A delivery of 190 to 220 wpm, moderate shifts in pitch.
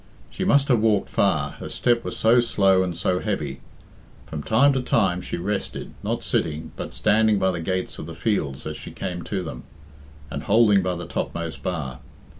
Yes: average, 195 wpm; average, 4.7 semitones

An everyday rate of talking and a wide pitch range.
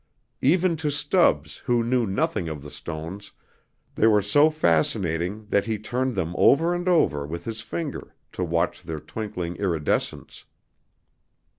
Yes: average, 145 wpm; wide, 8.4 semitones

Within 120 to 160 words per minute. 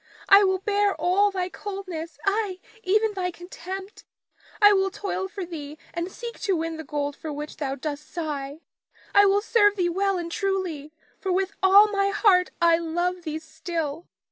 No: average, 175 wpm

